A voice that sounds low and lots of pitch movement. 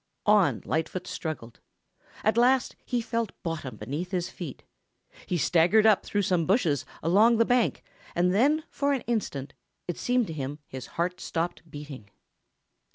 No: medium, 180 Hz; wide, 6.2 semitones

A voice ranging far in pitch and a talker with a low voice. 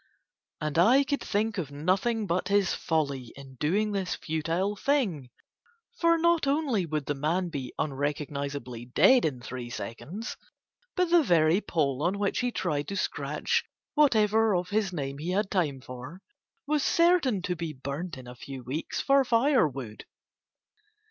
No: wide, 7.7 semitones; medium, 175 Hz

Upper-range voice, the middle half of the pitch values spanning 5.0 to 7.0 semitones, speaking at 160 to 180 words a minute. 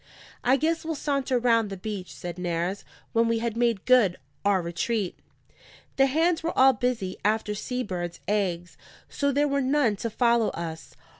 Yes: high, 230 Hz; wide, 5.5 semitones; average, 170 wpm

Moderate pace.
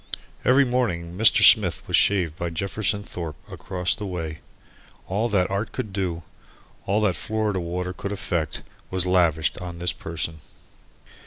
Yes: average, 150 wpm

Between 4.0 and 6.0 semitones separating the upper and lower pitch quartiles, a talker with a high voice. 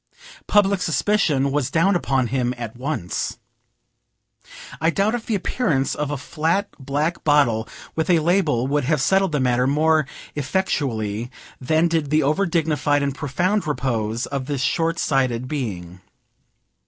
No: average, 4.4 semitones; medium, 145 Hz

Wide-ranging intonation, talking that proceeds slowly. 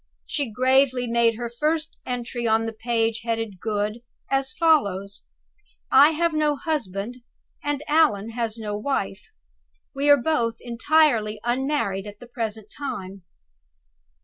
No: average, 4.6 semitones; slow, 130 wpm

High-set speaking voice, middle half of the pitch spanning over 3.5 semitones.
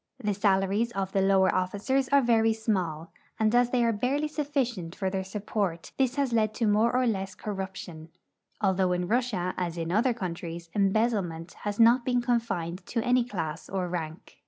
Yes: high, 205 Hz; average, 4.5 semitones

